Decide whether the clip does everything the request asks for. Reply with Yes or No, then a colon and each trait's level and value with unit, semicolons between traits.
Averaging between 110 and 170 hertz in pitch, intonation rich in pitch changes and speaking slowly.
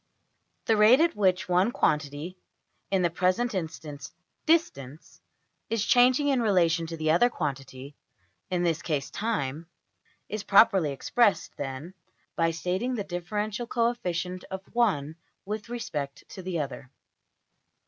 No: medium, 180 Hz; wide, 5.8 semitones; slow, 130 wpm